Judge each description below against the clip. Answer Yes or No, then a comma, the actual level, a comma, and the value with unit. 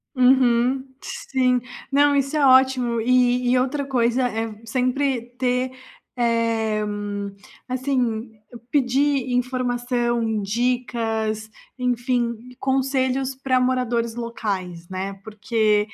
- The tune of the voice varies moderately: No, narrow, 2.1 semitones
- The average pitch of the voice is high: Yes, high, 245 Hz